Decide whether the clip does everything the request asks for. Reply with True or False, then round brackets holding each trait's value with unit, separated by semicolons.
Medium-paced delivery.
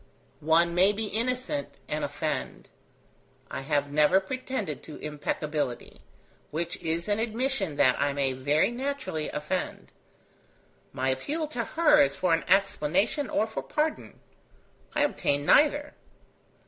False (130 wpm)